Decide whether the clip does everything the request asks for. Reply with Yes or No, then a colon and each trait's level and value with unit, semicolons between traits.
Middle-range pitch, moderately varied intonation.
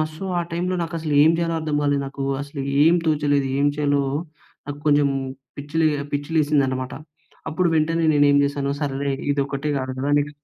No: medium, 145 Hz; narrow, 1.8 semitones